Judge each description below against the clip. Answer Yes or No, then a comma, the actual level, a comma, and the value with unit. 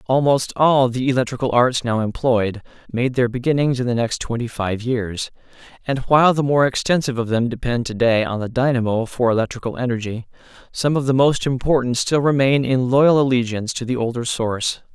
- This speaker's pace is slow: No, average, 185 wpm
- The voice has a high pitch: No, low, 125 Hz